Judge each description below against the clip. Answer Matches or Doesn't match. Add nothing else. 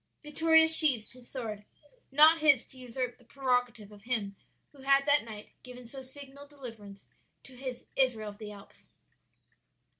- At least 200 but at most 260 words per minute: Doesn't match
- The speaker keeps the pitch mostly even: Doesn't match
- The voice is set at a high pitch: Matches